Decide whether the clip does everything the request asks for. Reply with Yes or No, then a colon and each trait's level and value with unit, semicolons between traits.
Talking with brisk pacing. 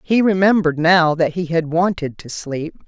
No: average, 190 wpm